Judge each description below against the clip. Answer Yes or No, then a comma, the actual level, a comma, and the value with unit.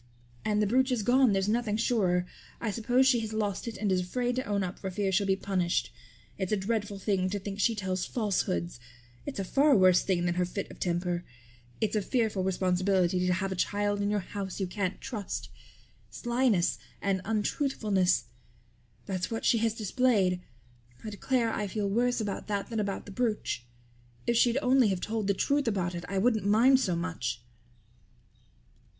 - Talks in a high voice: Yes, high, 205 Hz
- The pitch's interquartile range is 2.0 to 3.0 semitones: No, average, 3.4 semitones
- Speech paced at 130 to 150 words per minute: No, average, 190 wpm